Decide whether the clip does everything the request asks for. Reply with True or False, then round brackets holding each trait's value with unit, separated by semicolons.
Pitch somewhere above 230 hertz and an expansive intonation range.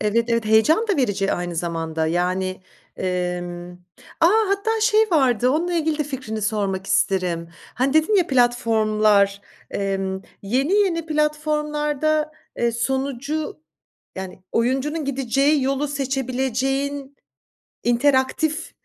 True (260 Hz; 7.3 semitones)